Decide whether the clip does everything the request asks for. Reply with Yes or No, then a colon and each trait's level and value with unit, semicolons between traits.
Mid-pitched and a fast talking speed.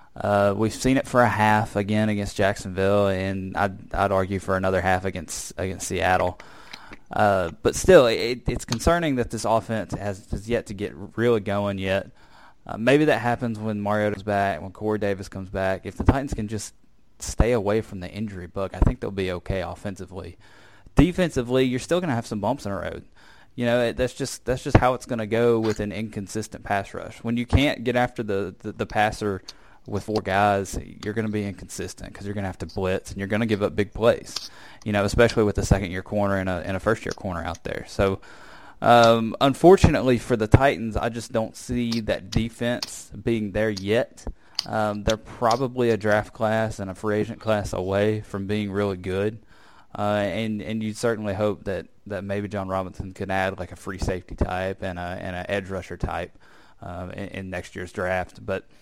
No: low, 105 Hz; fast, 210 wpm